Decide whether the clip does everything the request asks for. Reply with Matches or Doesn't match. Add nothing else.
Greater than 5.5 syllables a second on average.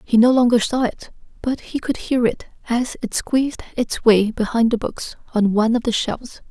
Doesn't match